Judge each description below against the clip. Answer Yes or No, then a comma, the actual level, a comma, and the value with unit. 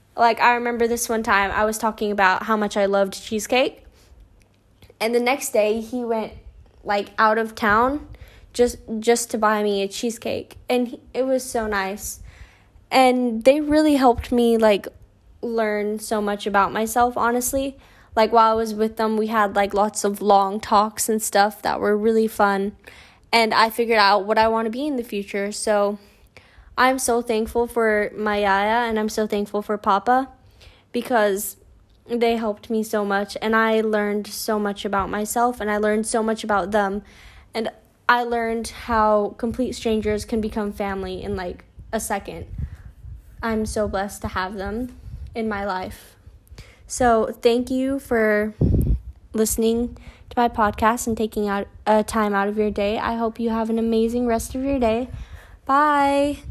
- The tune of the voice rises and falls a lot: No, narrow, 2.4 semitones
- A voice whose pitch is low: No, high, 220 Hz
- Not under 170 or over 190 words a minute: Yes, average, 175 wpm